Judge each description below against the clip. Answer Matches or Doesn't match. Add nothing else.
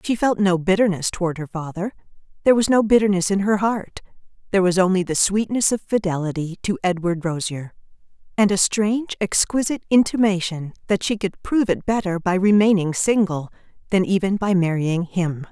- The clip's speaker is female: Matches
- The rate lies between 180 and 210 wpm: Doesn't match